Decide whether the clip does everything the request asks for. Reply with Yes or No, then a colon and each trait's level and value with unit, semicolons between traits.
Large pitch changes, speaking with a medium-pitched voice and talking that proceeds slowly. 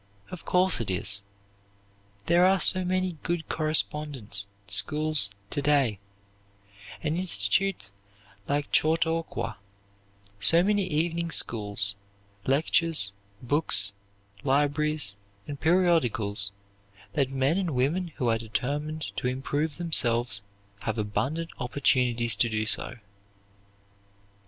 Yes: wide, 6.2 semitones; medium, 145 Hz; slow, 105 wpm